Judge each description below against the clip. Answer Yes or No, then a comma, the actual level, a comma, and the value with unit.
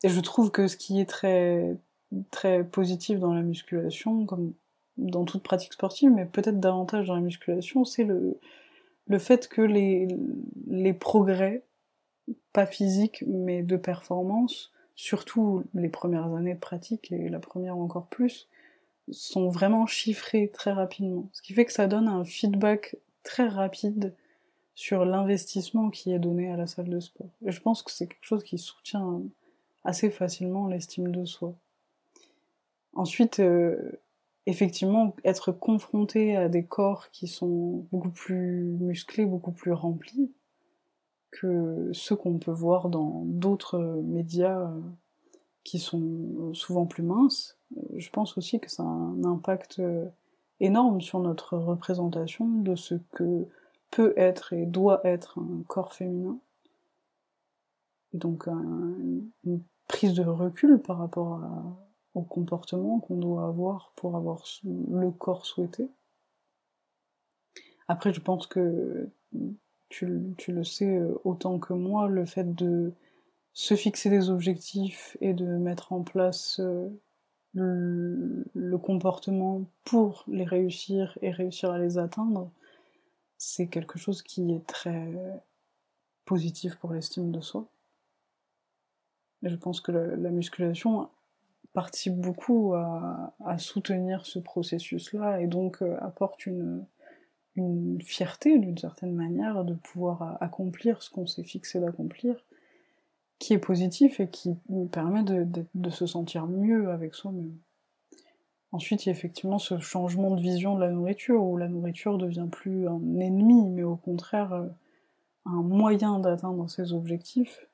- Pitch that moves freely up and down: No, average, 3.1 semitones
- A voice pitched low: No, medium, 185 Hz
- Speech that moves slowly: Yes, slow, 140 wpm